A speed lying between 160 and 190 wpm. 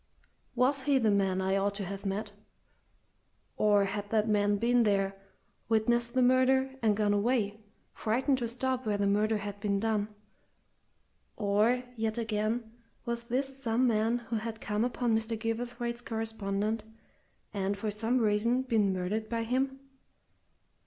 No: average, 150 wpm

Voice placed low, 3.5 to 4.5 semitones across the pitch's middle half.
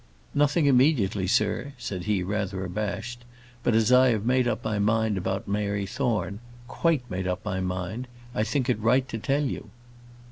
Yes: low, 110 Hz; average, 4.2 semitones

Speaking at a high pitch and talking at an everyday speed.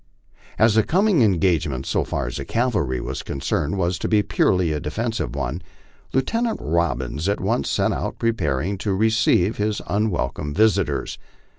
No: very low, 95 Hz; average, 160 wpm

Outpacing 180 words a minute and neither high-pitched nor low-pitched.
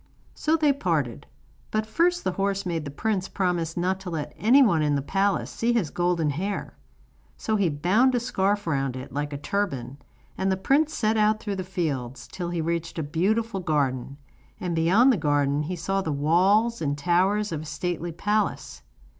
Yes: average, 190 wpm; medium, 180 Hz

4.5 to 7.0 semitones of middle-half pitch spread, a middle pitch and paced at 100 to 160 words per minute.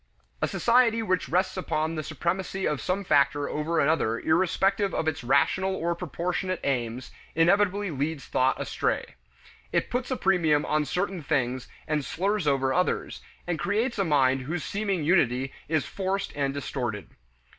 Yes: average, 5.2 semitones; medium, 165 Hz; average, 155 wpm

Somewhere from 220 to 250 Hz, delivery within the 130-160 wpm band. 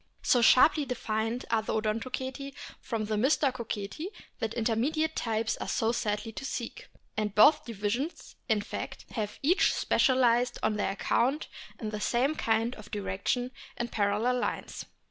Yes: high, 230 Hz; average, 145 wpm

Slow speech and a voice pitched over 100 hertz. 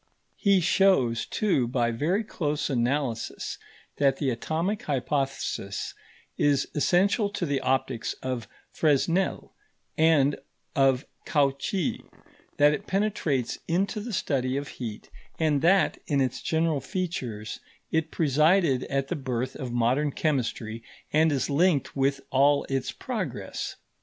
Yes: slow, 125 wpm; medium, 140 Hz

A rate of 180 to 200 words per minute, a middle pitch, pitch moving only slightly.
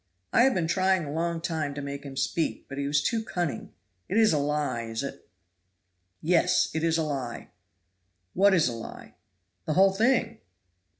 No: average, 185 wpm; medium, 160 Hz; average, 4.8 semitones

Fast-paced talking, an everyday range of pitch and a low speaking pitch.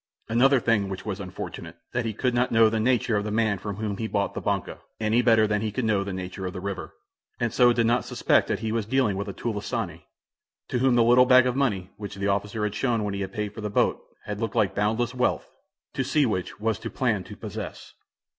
Yes: fast, 250 wpm; average, 3.0 semitones; low, 110 Hz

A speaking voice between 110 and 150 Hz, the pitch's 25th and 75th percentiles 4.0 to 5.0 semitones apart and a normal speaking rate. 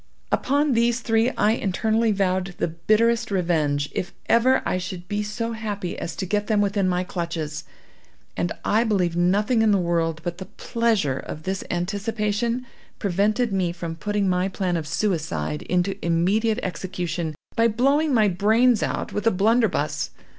No: high, 200 Hz; average, 4.3 semitones; average, 160 wpm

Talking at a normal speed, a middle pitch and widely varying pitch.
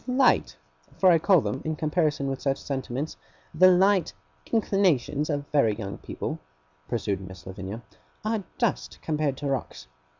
Yes: average, 155 wpm; medium, 145 Hz; wide, 6.2 semitones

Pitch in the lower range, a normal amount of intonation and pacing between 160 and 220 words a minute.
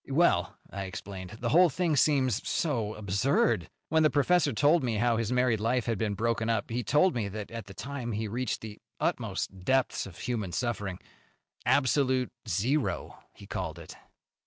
Yes: low, 115 Hz; average, 4.7 semitones; average, 175 wpm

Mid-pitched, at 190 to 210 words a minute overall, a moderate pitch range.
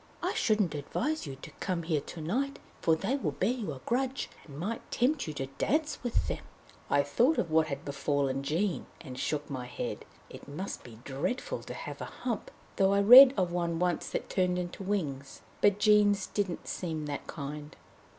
No: medium, 175 Hz; average, 195 wpm; wide, 6.5 semitones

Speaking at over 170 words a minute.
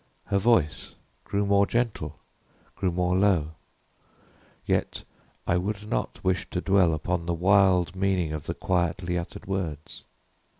No: slow, 135 wpm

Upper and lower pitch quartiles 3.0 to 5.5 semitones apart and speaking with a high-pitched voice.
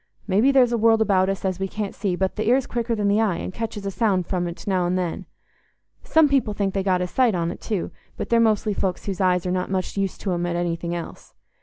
Yes: average, 3.4 semitones; high, 195 Hz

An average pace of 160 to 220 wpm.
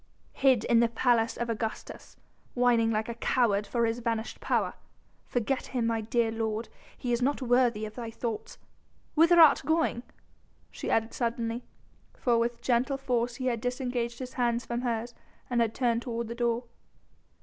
Yes: average, 170 wpm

